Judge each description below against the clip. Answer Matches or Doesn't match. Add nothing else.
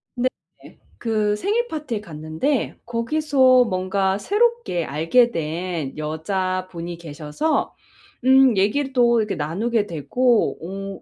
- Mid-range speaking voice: Doesn't match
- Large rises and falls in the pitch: Matches